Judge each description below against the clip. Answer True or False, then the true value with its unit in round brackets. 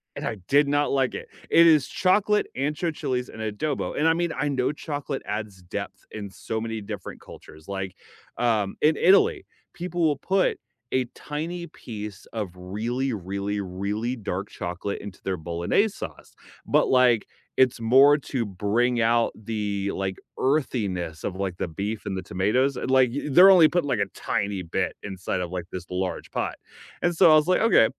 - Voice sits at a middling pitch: False (115 Hz)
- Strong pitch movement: True (6.9 semitones)